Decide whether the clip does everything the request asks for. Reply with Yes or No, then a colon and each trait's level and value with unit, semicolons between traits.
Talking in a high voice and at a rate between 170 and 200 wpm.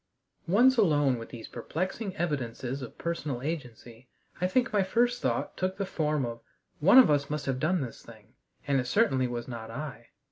No: medium, 145 Hz; average, 185 wpm